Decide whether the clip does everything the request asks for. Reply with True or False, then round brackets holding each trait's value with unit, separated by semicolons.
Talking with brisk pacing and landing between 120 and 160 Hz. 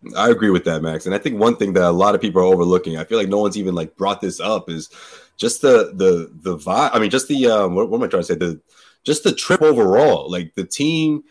False (270 wpm; 100 Hz)